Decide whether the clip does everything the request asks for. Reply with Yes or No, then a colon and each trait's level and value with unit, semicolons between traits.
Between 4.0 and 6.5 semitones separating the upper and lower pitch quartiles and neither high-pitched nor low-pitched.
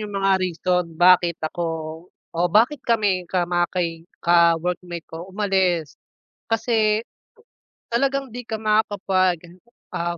No: average, 3.6 semitones; medium, 180 Hz